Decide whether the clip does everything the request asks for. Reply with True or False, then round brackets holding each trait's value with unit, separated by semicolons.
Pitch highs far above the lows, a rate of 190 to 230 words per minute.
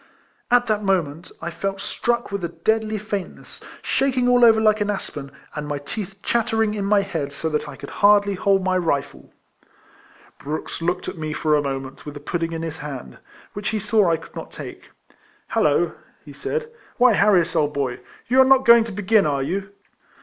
True (5.7 semitones; 195 wpm)